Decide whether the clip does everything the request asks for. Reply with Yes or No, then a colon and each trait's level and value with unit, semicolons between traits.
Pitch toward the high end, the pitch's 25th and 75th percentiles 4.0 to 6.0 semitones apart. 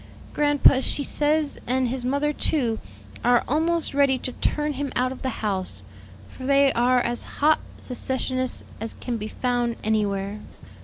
No: very high, 255 Hz; average, 3.0 semitones